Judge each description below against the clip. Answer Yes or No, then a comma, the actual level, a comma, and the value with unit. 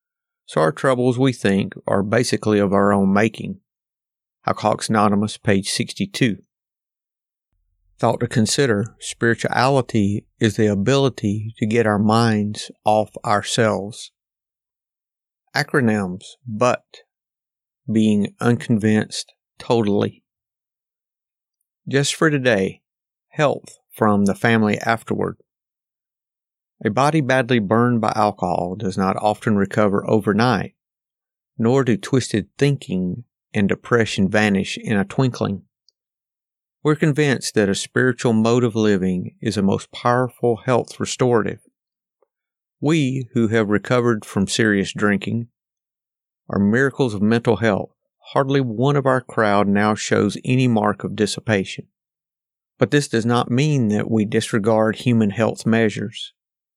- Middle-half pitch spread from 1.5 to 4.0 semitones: Yes, average, 3.4 semitones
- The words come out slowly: Yes, slow, 115 wpm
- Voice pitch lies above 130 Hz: No, low, 115 Hz